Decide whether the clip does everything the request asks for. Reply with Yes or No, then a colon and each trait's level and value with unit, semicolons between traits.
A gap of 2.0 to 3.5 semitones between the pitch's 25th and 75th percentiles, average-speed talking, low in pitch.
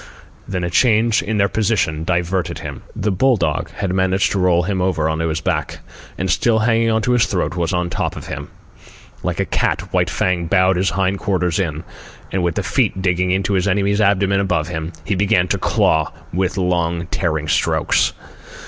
Yes: narrow, 2.4 semitones; average, 195 wpm; very low, 95 Hz